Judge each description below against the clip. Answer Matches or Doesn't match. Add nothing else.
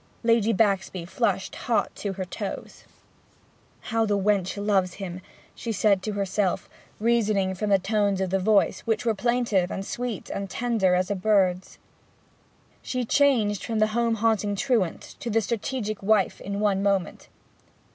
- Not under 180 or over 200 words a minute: Doesn't match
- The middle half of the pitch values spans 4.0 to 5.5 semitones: Doesn't match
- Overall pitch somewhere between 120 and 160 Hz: Doesn't match